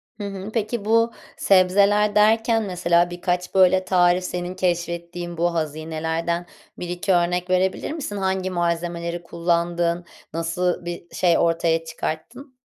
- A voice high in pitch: No, medium, 175 Hz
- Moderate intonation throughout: No, narrow, 1.9 semitones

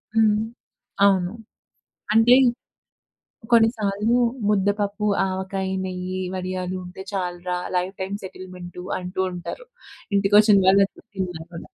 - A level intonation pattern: Yes, narrow, 2.0 semitones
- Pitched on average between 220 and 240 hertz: No, high, 190 Hz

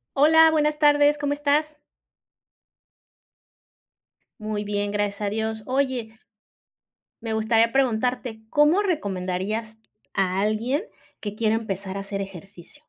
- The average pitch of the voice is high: Yes, high, 220 Hz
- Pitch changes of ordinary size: No, wide, 6.0 semitones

